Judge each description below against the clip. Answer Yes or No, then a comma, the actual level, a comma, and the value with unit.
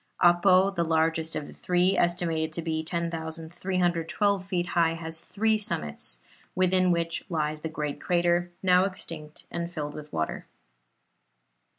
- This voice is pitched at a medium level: Yes, medium, 170 Hz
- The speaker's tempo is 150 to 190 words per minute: No, slow, 135 wpm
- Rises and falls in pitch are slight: Yes, narrow, 2.1 semitones